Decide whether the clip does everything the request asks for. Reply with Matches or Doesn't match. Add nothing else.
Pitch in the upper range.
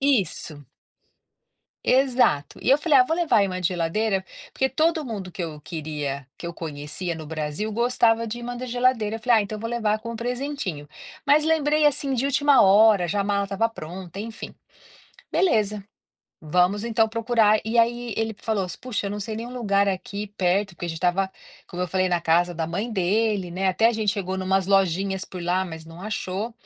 Matches